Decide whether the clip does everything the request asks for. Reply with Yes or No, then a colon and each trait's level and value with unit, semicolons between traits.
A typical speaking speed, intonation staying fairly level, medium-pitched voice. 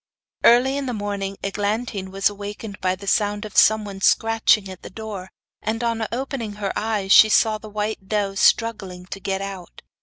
No: average, 180 wpm; narrow, 2.1 semitones; high, 205 Hz